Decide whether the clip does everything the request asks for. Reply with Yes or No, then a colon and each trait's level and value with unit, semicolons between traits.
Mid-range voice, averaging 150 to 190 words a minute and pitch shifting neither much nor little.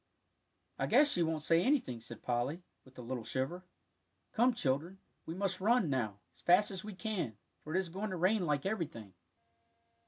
No: medium, 170 Hz; average, 185 wpm; wide, 7.1 semitones